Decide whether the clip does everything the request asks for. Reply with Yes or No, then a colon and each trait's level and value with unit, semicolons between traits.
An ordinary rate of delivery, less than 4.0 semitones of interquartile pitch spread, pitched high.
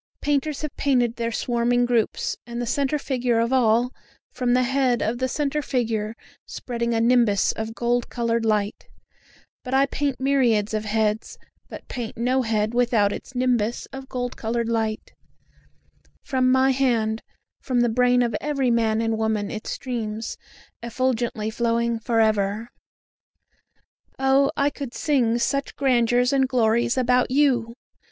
Yes: average, 150 wpm; narrow, 2.4 semitones; high, 240 Hz